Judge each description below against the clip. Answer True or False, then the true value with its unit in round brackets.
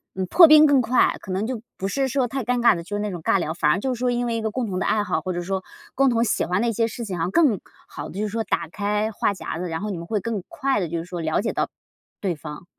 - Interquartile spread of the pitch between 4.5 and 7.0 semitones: True (5.0 semitones)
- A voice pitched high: True (210 Hz)